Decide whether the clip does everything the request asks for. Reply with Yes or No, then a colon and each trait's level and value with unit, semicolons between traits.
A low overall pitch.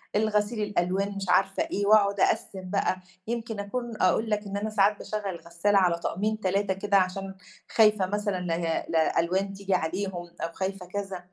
No: high, 195 Hz